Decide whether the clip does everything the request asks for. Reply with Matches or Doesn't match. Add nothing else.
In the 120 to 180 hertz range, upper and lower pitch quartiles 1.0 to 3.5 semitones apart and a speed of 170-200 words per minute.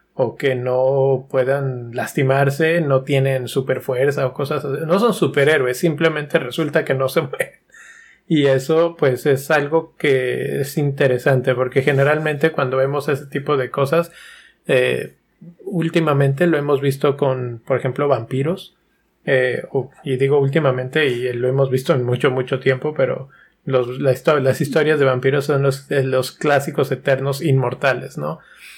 Doesn't match